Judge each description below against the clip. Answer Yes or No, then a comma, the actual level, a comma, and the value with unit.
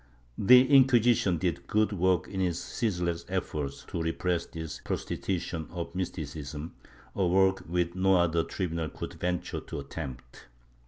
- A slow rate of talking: No, average, 145 wpm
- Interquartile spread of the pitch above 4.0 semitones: No, average, 2.8 semitones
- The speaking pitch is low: Yes, very low, 85 Hz